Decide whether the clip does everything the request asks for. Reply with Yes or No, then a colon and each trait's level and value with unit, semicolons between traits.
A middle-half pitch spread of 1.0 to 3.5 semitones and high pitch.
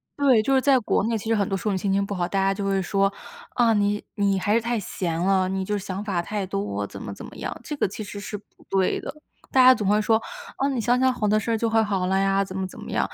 Yes: average, 2.7 semitones; high, 200 Hz